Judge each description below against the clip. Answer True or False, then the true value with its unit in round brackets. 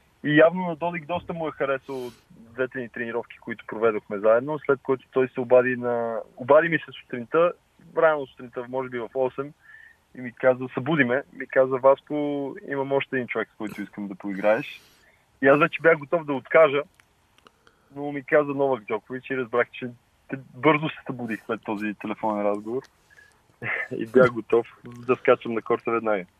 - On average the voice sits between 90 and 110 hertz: False (130 Hz)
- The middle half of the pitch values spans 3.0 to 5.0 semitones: True (3.6 semitones)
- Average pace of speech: False (175 wpm)